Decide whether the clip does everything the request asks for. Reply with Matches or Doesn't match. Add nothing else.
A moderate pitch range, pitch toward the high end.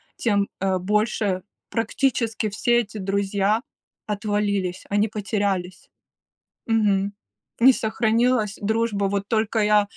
Doesn't match